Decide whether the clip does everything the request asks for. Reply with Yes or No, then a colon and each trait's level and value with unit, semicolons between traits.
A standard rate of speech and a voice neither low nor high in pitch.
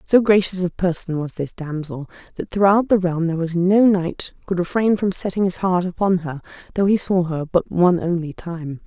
No: fast, 210 wpm; medium, 180 Hz